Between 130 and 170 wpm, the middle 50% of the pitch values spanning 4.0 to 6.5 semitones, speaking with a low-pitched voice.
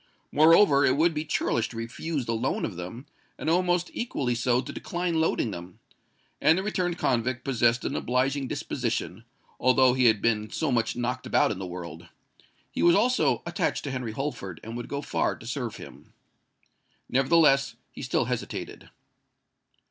Yes: average, 165 wpm; average, 5.3 semitones; low, 130 Hz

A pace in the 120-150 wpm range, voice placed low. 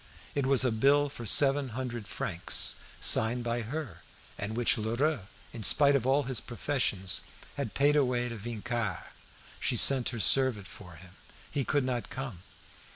No: average, 160 wpm; low, 120 Hz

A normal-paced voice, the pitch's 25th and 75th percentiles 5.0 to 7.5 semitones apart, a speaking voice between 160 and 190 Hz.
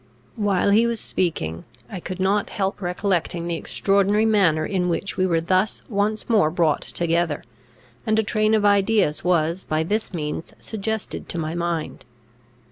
No: average, 160 wpm; average, 3.7 semitones; medium, 185 Hz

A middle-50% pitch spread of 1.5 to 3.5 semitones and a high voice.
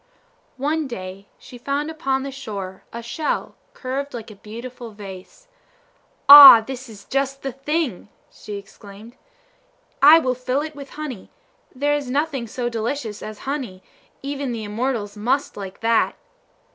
No: average, 4.6 semitones; very high, 250 Hz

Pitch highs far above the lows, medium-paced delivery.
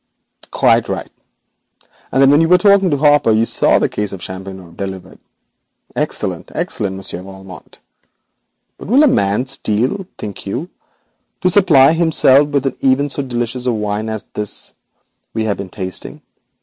Yes: wide, 6.6 semitones; average, 155 wpm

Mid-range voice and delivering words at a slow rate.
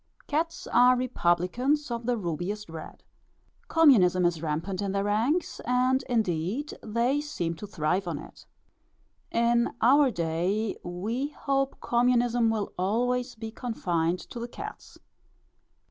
No: high, 225 Hz; slow, 130 wpm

